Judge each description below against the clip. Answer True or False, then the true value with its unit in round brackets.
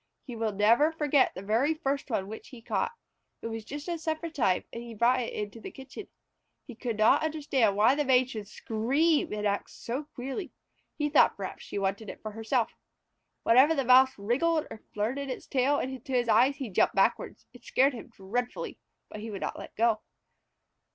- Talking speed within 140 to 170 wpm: False (195 wpm)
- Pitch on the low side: False (250 Hz)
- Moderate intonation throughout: True (4.4 semitones)